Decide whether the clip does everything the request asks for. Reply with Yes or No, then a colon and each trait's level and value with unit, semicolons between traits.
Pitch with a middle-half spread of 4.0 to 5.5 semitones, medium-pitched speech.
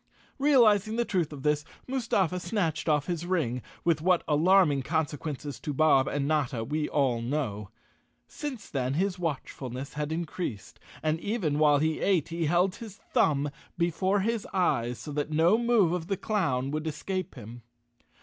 Yes: average, 4.7 semitones; medium, 160 Hz